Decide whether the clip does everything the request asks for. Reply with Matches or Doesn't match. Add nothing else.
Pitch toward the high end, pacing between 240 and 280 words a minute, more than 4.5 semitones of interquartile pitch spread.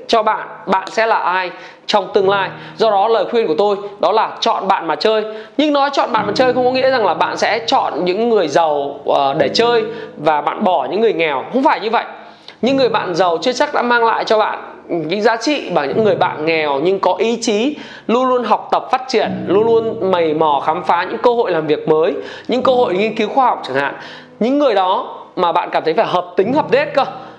Matches